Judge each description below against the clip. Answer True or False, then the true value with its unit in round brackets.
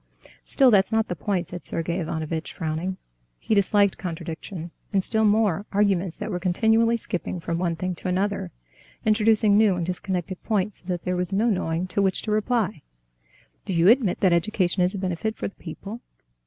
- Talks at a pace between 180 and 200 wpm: True (185 wpm)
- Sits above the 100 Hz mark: True (190 Hz)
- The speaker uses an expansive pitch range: False (3.3 semitones)